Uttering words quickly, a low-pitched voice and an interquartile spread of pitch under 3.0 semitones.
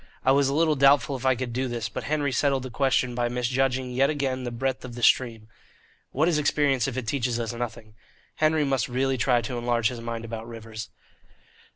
Yes: fast, 215 wpm; low, 130 Hz; narrow, 2.4 semitones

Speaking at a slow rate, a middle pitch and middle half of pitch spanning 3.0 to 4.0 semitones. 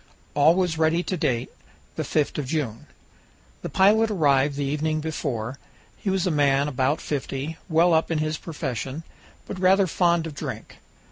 No: average, 165 wpm; medium, 155 Hz; average, 3.5 semitones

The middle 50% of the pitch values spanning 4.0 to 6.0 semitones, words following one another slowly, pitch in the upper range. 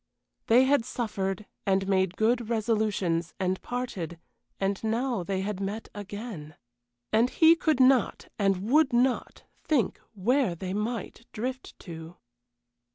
Yes: average, 4.4 semitones; slow, 130 wpm; high, 215 Hz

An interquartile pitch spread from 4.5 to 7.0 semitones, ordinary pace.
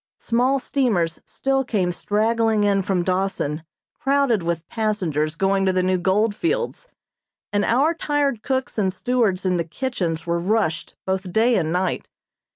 Yes: average, 5.2 semitones; average, 155 wpm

